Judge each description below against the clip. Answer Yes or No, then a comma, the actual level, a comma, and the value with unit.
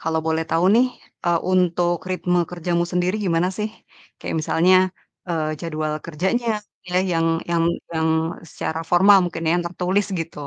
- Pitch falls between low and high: Yes, medium, 175 Hz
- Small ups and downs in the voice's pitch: Yes, narrow, 1.9 semitones